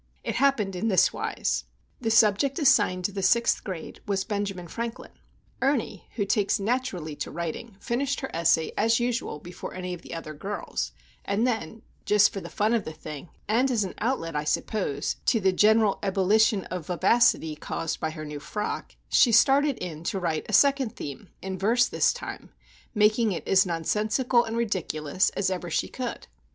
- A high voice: Yes, high, 200 Hz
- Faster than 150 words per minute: Yes, average, 180 wpm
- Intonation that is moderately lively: Yes, average, 4.7 semitones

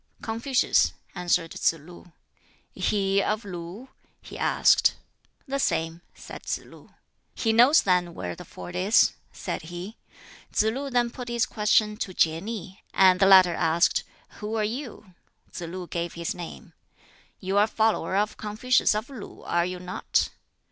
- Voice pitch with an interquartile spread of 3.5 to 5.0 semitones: Yes, average, 4.1 semitones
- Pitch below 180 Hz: No, high, 195 Hz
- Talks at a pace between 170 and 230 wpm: No, average, 160 wpm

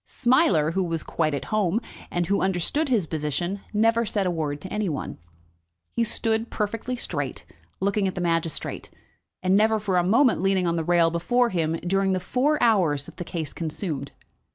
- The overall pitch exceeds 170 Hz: Yes, medium, 185 Hz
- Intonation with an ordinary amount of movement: Yes, average, 4.7 semitones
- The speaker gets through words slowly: No, average, 185 wpm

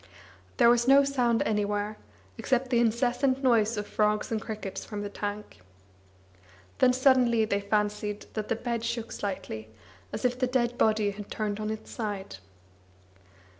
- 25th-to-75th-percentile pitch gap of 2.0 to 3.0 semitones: Yes, average, 2.7 semitones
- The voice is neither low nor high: No, high, 220 Hz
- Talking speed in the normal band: Yes, average, 155 wpm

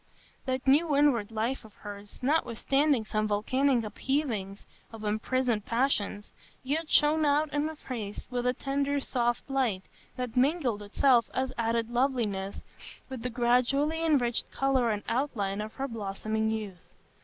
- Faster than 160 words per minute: No, average, 145 wpm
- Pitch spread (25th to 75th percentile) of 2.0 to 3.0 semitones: No, average, 4.2 semitones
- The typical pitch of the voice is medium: No, high, 245 Hz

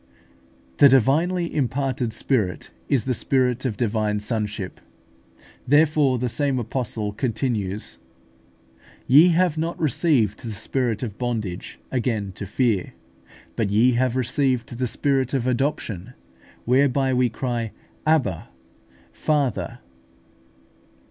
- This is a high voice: No, low, 125 Hz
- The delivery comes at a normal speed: No, slow, 115 wpm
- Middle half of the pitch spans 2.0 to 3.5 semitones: No, average, 4.2 semitones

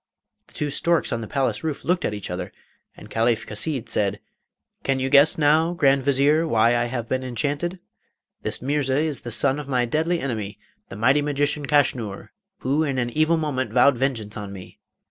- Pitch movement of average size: Yes, average, 4.1 semitones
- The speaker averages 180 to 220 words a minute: Yes, average, 190 wpm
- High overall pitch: No, low, 135 Hz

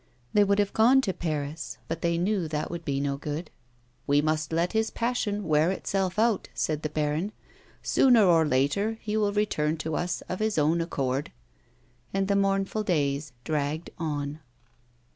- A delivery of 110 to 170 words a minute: No, average, 180 wpm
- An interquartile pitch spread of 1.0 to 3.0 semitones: No, average, 5.1 semitones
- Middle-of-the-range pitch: Yes, medium, 165 Hz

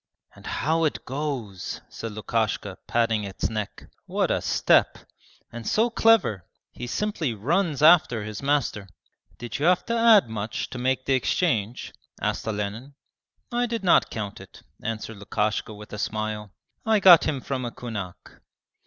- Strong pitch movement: Yes, wide, 6.7 semitones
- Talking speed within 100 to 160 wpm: Yes, average, 155 wpm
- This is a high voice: No, low, 120 Hz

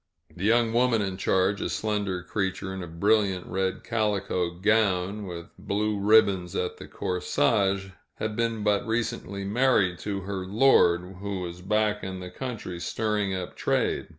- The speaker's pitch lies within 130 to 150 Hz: No, low, 100 Hz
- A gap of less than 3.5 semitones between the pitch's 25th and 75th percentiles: Yes, narrow, 2.6 semitones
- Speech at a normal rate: Yes, average, 155 wpm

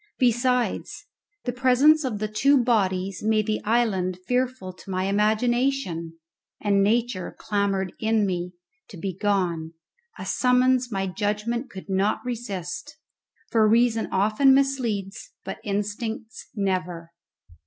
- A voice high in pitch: Yes, high, 215 Hz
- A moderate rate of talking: No, slow, 120 wpm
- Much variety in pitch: No, average, 4.2 semitones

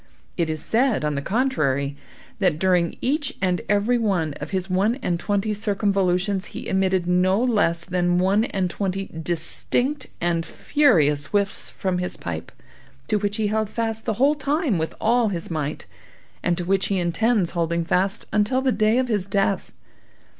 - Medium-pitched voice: No, high, 195 Hz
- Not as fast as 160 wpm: No, average, 170 wpm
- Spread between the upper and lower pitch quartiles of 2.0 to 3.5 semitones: No, average, 4.0 semitones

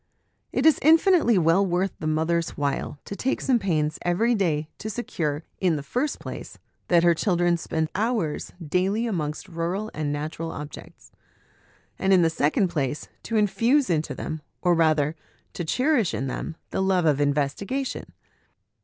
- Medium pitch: Yes, medium, 175 Hz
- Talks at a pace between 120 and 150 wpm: No, average, 160 wpm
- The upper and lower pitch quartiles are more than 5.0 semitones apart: Yes, wide, 5.5 semitones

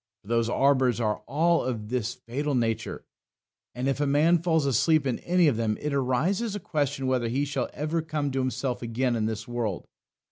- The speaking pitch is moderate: No, low, 130 Hz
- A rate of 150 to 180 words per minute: No, average, 200 wpm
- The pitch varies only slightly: No, average, 4.0 semitones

